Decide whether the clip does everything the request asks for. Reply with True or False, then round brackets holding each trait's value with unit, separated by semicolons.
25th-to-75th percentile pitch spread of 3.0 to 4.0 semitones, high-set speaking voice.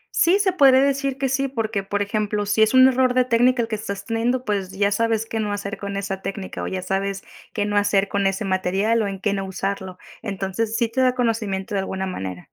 True (3.3 semitones; 205 Hz)